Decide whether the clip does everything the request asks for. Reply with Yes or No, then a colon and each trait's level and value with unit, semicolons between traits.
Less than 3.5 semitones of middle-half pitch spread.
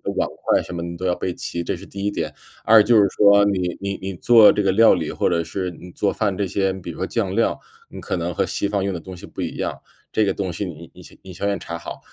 Yes: narrow, 2.6 semitones